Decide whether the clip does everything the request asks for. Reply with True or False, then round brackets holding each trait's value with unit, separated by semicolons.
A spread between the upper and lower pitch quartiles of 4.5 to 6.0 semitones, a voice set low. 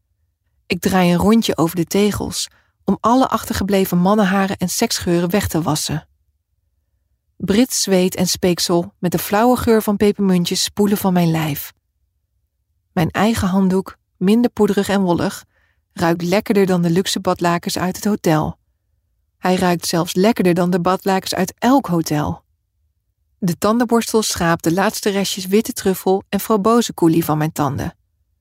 False (5.3 semitones; 180 Hz)